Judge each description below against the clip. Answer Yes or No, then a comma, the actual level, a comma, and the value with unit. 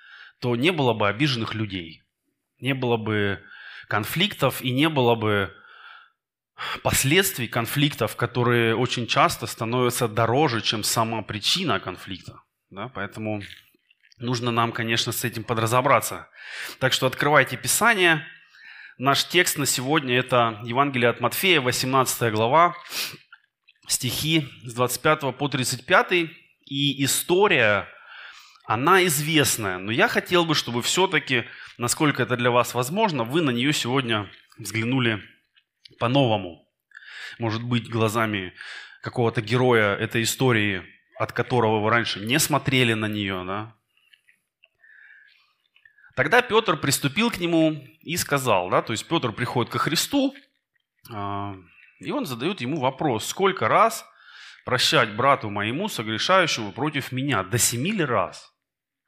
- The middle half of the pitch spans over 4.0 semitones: Yes, average, 4.6 semitones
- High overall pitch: No, low, 125 Hz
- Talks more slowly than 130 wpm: Yes, average, 120 wpm